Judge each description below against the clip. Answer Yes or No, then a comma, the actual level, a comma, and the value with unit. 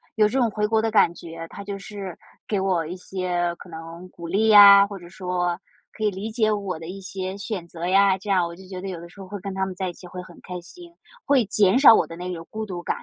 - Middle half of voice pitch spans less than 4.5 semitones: Yes, narrow, 2.6 semitones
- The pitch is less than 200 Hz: Yes, high, 190 Hz